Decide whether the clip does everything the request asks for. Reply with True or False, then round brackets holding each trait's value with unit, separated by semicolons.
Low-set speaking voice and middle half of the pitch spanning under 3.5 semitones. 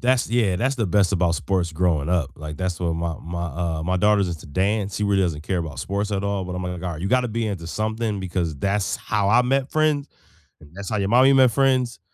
False (95 Hz; 4.3 semitones)